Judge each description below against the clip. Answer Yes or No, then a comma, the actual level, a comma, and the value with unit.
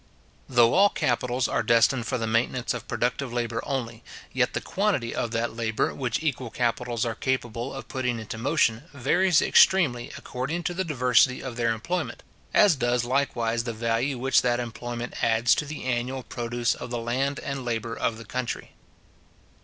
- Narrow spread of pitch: Yes, narrow, 2.3 semitones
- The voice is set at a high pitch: No, low, 120 Hz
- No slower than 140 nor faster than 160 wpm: No, average, 175 wpm